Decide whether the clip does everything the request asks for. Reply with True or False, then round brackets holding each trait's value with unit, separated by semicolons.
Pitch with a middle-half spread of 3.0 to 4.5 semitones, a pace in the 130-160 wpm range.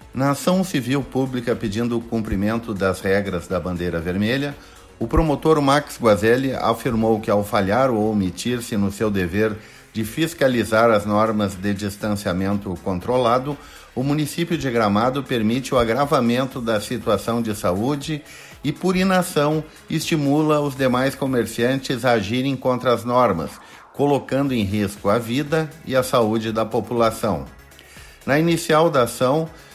False (5.0 semitones; 140 wpm)